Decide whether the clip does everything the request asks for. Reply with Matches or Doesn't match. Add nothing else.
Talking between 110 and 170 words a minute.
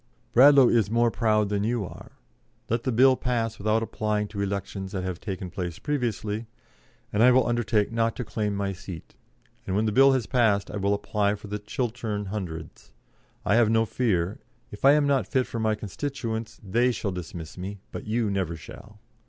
Doesn't match